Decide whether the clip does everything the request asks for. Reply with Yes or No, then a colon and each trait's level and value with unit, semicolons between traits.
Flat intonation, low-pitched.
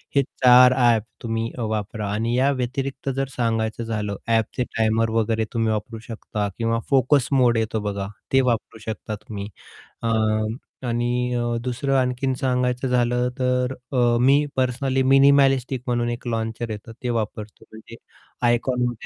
Yes: narrow, 2.1 semitones; low, 120 Hz